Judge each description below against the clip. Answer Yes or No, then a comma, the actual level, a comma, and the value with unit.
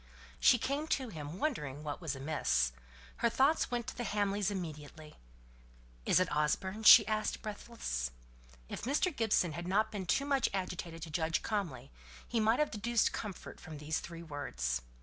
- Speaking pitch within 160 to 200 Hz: Yes, high, 190 Hz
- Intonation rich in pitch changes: Yes, wide, 6.8 semitones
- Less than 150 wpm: No, average, 170 wpm